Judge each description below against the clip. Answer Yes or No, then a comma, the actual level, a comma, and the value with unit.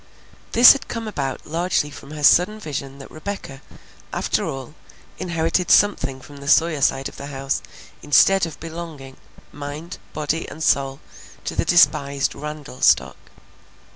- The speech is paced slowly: No, average, 145 wpm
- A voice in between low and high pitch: Yes, medium, 150 Hz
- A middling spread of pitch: Yes, average, 3.5 semitones